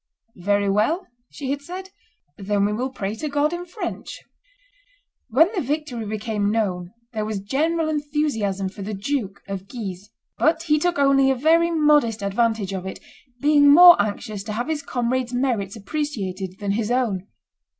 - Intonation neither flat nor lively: No, wide, 6.6 semitones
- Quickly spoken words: No, average, 165 wpm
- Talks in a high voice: Yes, high, 240 Hz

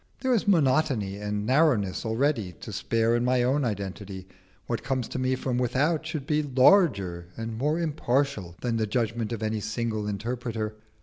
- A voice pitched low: Yes, low, 120 Hz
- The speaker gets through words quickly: No, average, 170 wpm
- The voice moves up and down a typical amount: Yes, average, 4.5 semitones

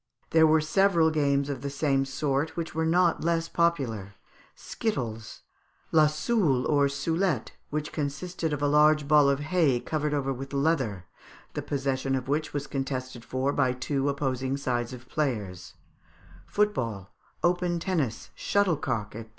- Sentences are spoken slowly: No, average, 150 wpm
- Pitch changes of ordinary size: Yes, average, 3.5 semitones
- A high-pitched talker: No, medium, 140 Hz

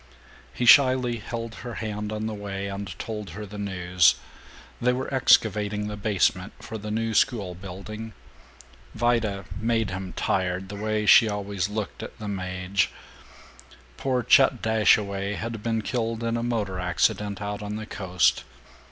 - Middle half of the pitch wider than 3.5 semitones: No, narrow, 2.4 semitones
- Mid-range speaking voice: No, low, 105 Hz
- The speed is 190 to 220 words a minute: No, average, 150 wpm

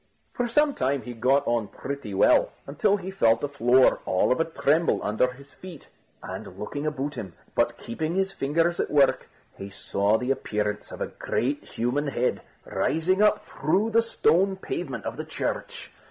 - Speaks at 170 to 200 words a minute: Yes, average, 180 wpm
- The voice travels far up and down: Yes, wide, 6.6 semitones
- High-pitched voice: No, medium, 140 Hz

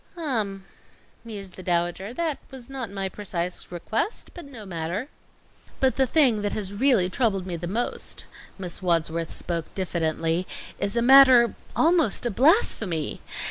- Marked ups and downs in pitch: Yes, wide, 6.3 semitones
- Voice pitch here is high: Yes, high, 200 Hz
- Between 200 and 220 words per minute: No, average, 145 wpm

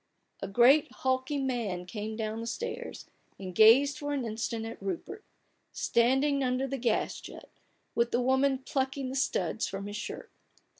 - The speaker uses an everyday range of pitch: Yes, average, 3.6 semitones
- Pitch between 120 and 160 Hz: No, very high, 250 Hz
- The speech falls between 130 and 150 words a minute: No, average, 170 wpm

